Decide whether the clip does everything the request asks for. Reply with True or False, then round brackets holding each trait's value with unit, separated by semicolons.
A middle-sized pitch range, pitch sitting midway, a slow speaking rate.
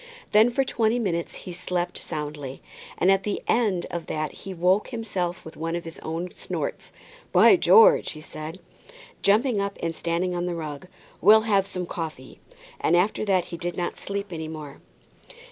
False (3.5 semitones; 180 Hz; 180 wpm)